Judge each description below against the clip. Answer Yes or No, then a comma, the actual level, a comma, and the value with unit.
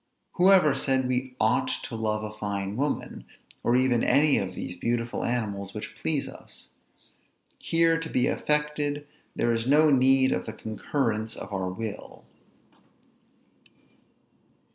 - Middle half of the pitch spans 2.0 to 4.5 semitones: No, average, 5.0 semitones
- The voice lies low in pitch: Yes, low, 125 Hz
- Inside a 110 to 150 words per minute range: Yes, average, 140 wpm